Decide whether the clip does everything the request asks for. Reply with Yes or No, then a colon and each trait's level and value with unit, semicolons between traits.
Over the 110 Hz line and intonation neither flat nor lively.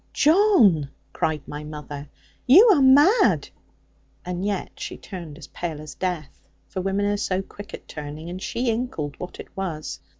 No: medium, 185 Hz; wide, 7.2 semitones